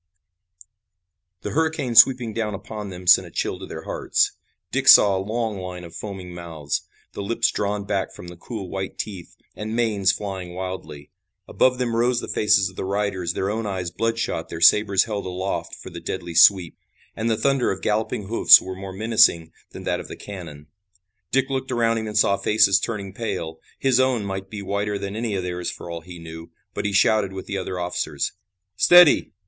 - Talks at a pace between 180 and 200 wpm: Yes, average, 195 wpm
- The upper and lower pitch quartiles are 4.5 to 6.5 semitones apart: No, average, 3.4 semitones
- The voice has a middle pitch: No, low, 100 Hz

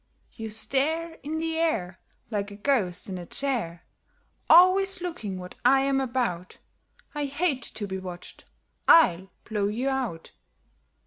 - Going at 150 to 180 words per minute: No, average, 140 wpm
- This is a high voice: Yes, very high, 250 Hz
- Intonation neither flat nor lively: No, wide, 8.0 semitones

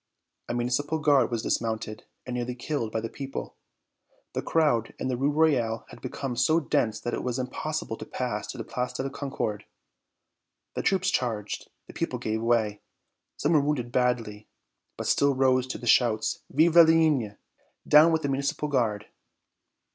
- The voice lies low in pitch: Yes, low, 125 Hz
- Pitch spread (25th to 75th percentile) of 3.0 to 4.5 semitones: Yes, average, 4.1 semitones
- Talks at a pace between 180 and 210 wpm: No, average, 170 wpm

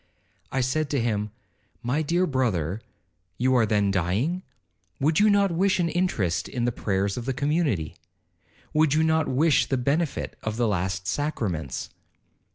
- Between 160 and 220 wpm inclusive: No, average, 150 wpm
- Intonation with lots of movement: Yes, wide, 7.9 semitones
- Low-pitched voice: Yes, low, 125 Hz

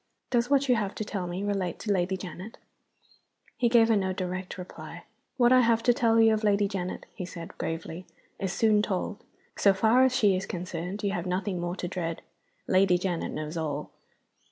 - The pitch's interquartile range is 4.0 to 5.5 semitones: No, average, 3.6 semitones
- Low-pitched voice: No, high, 195 Hz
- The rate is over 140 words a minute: Yes, average, 200 wpm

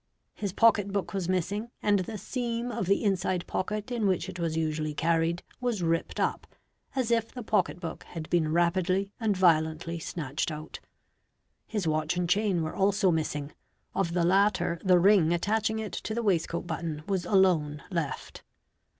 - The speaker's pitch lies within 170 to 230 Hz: Yes, medium, 185 Hz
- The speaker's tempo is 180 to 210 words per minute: No, average, 165 wpm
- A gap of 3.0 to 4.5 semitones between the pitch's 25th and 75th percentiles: Yes, average, 3.8 semitones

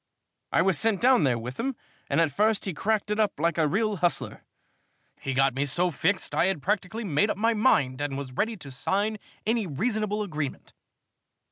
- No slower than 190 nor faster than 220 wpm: Yes, fast, 205 wpm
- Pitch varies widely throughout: Yes, wide, 6.9 semitones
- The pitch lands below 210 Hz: Yes, high, 190 Hz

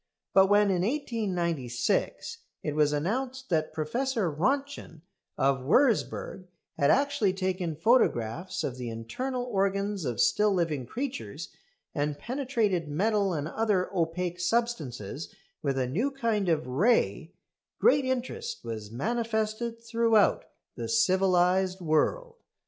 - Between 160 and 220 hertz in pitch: Yes, high, 190 Hz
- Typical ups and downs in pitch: No, wide, 7.2 semitones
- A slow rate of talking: Yes, slow, 120 wpm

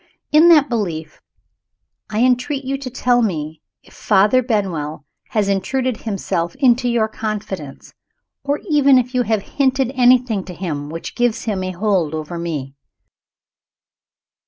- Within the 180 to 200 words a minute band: No, average, 140 wpm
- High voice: Yes, high, 220 Hz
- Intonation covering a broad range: Yes, wide, 6.5 semitones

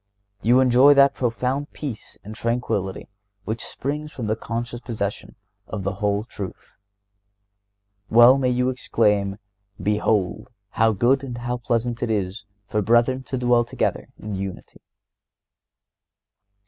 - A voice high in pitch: No, low, 115 Hz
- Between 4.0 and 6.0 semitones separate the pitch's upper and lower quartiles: No, average, 3.1 semitones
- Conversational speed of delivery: No, slow, 130 wpm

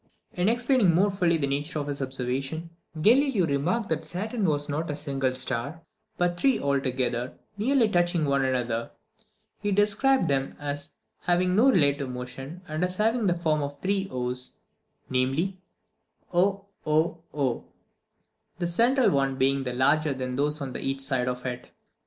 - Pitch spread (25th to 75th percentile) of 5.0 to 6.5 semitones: Yes, wide, 5.5 semitones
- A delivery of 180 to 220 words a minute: No, average, 150 wpm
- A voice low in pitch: No, medium, 150 Hz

